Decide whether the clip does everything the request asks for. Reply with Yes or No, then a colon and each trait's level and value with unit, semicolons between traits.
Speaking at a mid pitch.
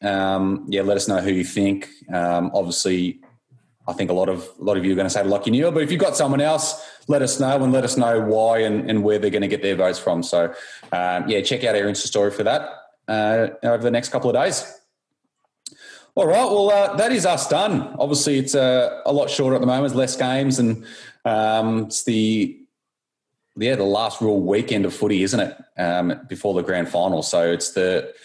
No: low, 110 Hz